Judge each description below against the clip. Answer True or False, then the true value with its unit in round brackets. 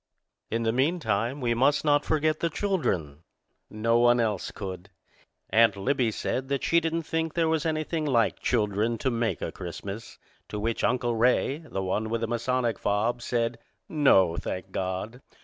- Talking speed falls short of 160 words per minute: False (165 wpm)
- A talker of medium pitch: False (120 Hz)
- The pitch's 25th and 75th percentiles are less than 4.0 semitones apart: False (5.3 semitones)